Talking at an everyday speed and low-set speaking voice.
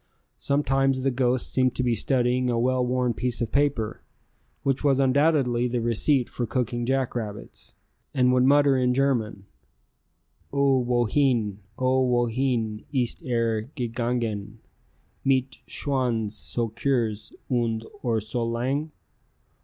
No: slow, 125 wpm; low, 125 Hz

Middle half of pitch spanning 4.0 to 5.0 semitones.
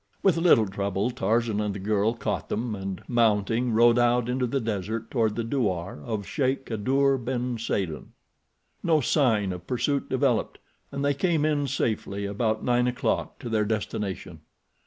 No: average, 3.6 semitones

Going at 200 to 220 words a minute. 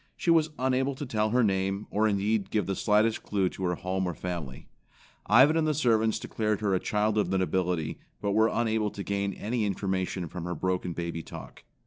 Yes: fast, 205 wpm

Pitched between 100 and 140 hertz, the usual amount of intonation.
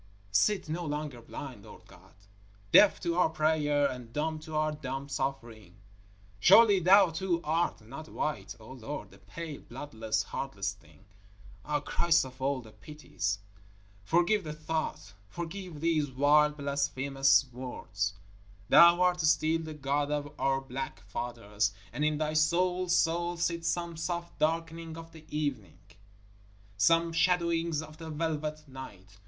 No: medium, 150 Hz; average, 4.0 semitones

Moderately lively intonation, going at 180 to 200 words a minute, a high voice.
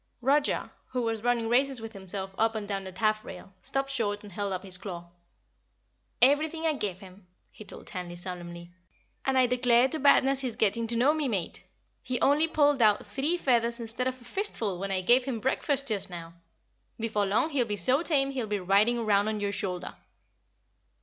Yes: average, 5.0 semitones; average, 195 wpm; high, 225 Hz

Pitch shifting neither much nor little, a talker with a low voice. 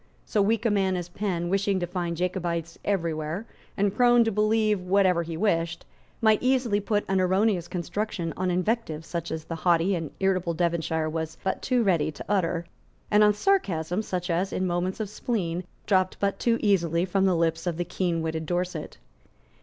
No: average, 3.4 semitones; medium, 180 Hz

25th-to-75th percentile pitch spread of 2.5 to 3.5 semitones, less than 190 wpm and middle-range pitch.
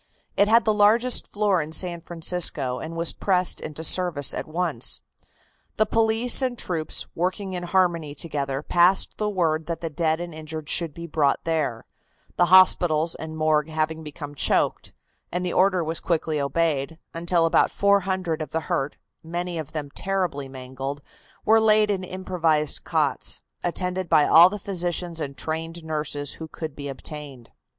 Yes: average, 3.2 semitones; average, 165 wpm; medium, 165 Hz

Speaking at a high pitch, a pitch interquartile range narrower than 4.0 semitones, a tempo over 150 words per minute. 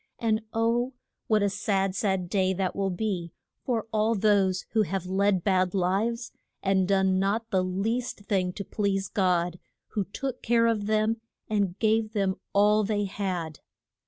Yes: high, 200 Hz; narrow, 2.5 semitones; average, 160 wpm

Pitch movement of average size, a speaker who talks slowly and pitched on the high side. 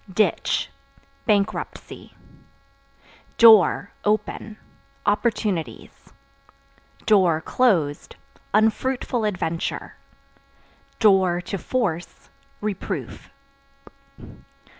Yes: average, 3.7 semitones; slow, 45 wpm; high, 205 Hz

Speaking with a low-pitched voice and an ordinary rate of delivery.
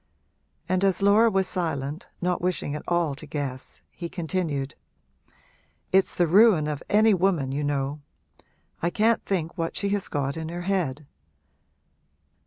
No: medium, 170 Hz; average, 150 wpm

